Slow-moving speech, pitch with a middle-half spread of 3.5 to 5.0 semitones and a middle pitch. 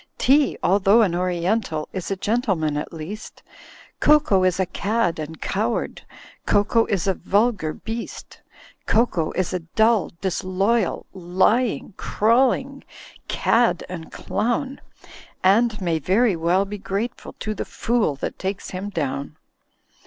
No: slow, 130 wpm; average, 4.5 semitones; high, 195 Hz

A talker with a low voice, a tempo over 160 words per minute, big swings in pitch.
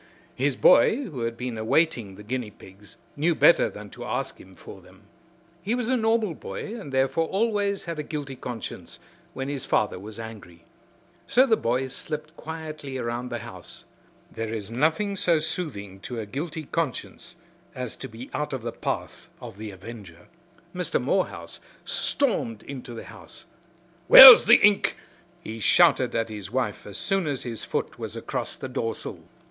Yes: low, 130 Hz; average, 170 wpm; wide, 6.9 semitones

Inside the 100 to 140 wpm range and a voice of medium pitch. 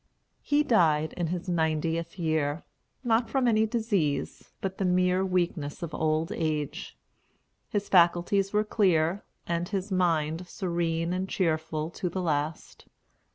Yes: slow, 135 wpm; medium, 175 Hz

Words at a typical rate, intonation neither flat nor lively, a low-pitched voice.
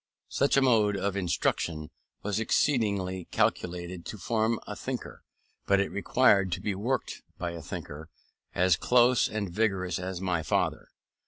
Yes: average, 150 wpm; average, 3.7 semitones; low, 100 Hz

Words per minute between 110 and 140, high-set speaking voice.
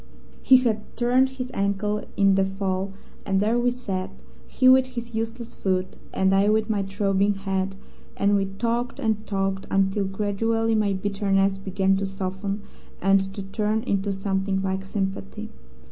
No: average, 160 wpm; high, 200 Hz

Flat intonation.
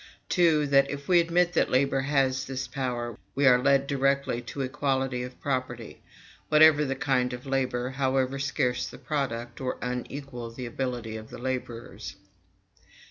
Yes: narrow, 1.9 semitones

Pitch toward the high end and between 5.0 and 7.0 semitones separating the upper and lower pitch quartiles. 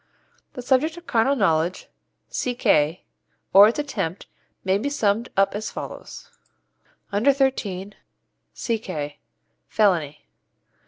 Yes: high, 205 Hz; wide, 5.5 semitones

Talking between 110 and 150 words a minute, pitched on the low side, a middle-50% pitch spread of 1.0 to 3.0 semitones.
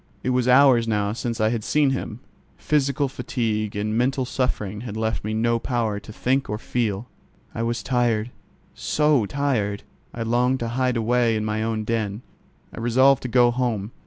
No: average, 180 wpm; low, 115 Hz; average, 2.7 semitones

